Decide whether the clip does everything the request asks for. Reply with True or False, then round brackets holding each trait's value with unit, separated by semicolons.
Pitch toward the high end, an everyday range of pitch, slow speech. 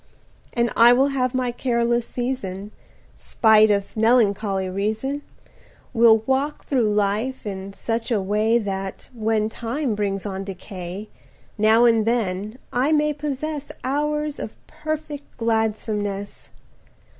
True (225 Hz; 3.9 semitones; 125 wpm)